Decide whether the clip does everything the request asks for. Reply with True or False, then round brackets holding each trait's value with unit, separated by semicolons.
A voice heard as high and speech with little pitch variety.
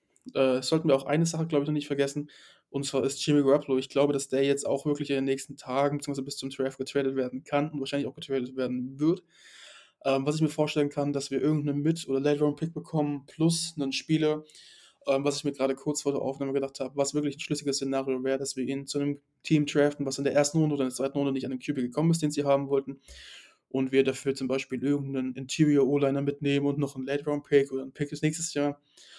False (140 Hz; 1.6 semitones)